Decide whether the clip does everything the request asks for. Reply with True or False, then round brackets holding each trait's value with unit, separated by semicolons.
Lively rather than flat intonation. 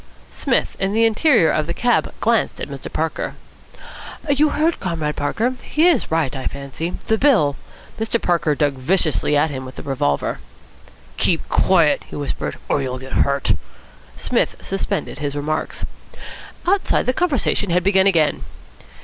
True (7.7 semitones)